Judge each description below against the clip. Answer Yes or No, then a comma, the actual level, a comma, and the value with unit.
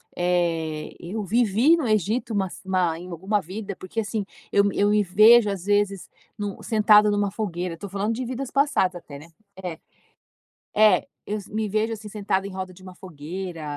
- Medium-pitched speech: No, high, 200 Hz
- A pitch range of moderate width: Yes, average, 3.0 semitones